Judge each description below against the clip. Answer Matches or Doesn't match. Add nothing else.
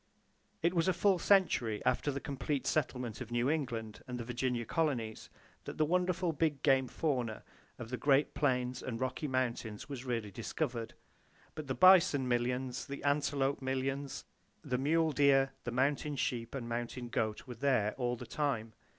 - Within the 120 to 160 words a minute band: Doesn't match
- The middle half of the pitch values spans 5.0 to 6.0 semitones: Doesn't match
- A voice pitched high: Doesn't match